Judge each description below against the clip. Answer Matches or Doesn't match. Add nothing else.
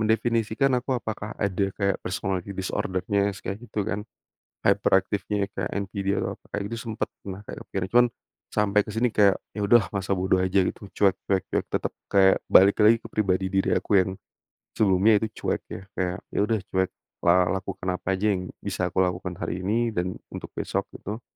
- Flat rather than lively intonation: Matches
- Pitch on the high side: Doesn't match